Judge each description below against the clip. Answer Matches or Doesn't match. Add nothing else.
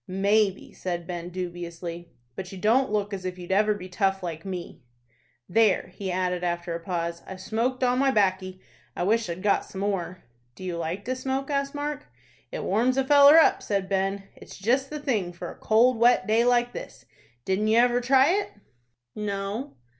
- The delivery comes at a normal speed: Matches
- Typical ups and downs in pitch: Matches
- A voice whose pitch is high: Matches